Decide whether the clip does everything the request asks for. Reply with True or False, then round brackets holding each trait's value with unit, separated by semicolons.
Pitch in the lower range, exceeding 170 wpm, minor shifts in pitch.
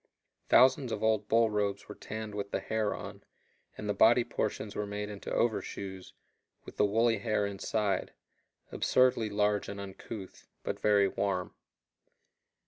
False (105 Hz; 145 wpm; 1.6 semitones)